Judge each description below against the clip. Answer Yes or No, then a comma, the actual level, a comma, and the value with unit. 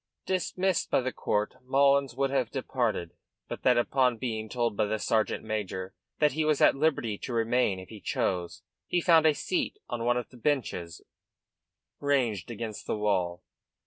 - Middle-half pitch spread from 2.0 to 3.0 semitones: No, average, 4.5 semitones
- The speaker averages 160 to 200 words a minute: Yes, average, 175 wpm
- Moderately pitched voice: No, low, 120 Hz